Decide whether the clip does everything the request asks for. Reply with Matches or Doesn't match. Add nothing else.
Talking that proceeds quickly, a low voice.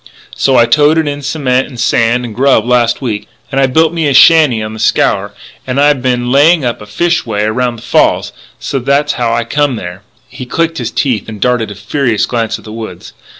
Matches